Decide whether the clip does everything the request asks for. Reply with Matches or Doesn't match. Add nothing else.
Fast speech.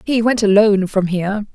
Doesn't match